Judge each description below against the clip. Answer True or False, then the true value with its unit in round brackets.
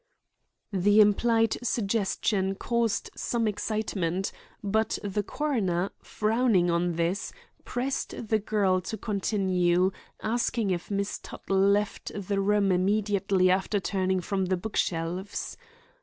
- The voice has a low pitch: False (200 Hz)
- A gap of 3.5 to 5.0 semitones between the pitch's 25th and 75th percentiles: False (2.6 semitones)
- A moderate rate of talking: False (115 wpm)